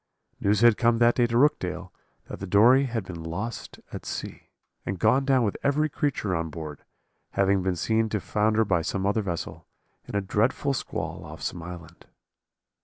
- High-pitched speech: No, low, 105 Hz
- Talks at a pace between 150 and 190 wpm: Yes, average, 180 wpm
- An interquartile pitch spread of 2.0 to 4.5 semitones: No, average, 4.9 semitones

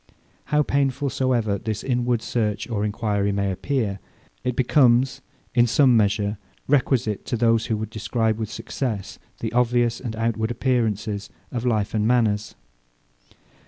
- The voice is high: No, low, 115 Hz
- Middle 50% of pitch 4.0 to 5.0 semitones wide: No, average, 2.7 semitones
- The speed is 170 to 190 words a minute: No, average, 140 wpm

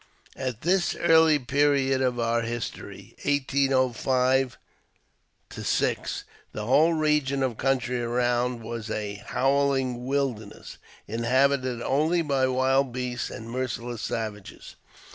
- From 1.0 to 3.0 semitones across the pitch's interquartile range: Yes, narrow, 2.6 semitones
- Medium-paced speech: No, slow, 110 wpm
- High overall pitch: No, low, 130 Hz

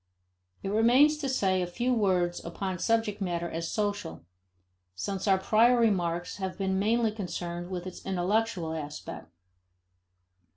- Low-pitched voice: No, high, 190 Hz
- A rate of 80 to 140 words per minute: Yes, slow, 135 wpm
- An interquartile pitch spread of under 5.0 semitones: Yes, average, 4.0 semitones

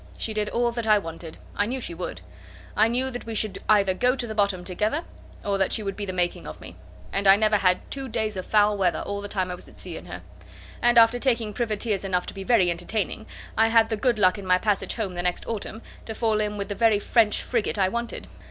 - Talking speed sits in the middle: No, fast, 255 wpm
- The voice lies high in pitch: Yes, high, 210 Hz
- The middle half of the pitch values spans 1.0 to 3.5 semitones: Yes, average, 3.0 semitones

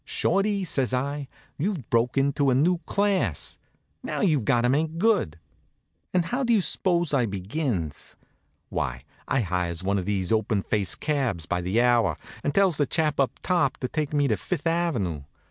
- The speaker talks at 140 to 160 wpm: No, average, 180 wpm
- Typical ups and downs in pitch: No, wide, 8.6 semitones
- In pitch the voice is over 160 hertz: No, low, 135 Hz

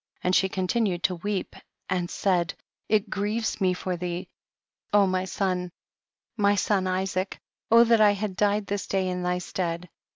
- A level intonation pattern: Yes, narrow, 2.1 semitones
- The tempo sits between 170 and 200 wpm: No, average, 160 wpm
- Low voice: No, high, 190 Hz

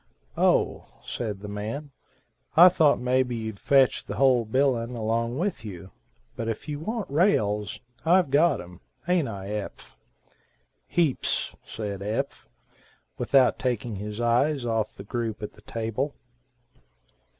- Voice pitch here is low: Yes, low, 120 Hz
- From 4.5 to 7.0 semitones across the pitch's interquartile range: Yes, average, 4.9 semitones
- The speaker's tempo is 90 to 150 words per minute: Yes, slow, 135 wpm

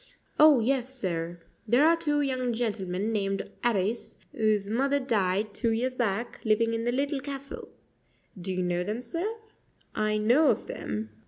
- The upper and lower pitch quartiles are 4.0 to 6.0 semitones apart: Yes, average, 5.0 semitones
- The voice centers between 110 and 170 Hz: No, high, 230 Hz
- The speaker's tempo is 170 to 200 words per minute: No, average, 160 wpm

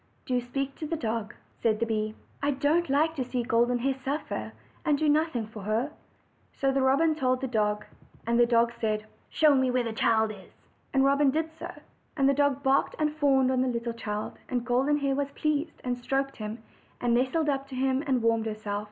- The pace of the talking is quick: Yes, fast, 210 wpm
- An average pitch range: Yes, average, 3.4 semitones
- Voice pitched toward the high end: Yes, very high, 260 Hz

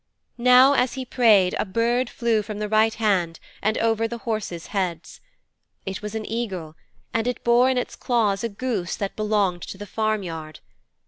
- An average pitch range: Yes, average, 3.3 semitones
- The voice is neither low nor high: No, high, 215 Hz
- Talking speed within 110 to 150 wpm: No, average, 180 wpm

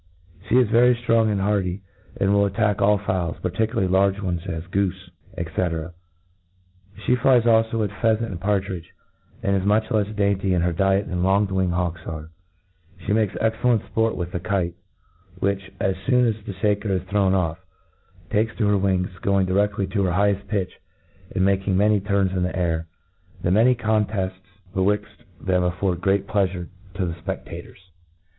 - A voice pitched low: Yes, low, 100 Hz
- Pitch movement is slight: Yes, narrow, 2.3 semitones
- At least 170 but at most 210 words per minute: Yes, average, 175 wpm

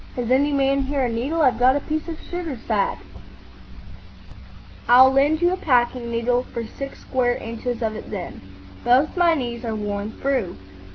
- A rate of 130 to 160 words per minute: No, average, 175 wpm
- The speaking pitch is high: Yes, very high, 255 Hz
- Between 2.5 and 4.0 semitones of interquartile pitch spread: Yes, average, 3.3 semitones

